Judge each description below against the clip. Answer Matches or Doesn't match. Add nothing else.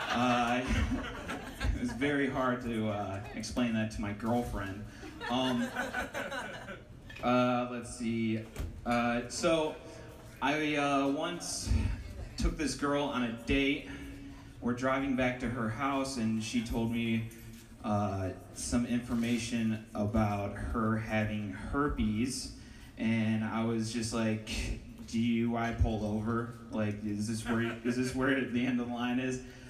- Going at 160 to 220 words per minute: Doesn't match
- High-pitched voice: Doesn't match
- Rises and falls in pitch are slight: Matches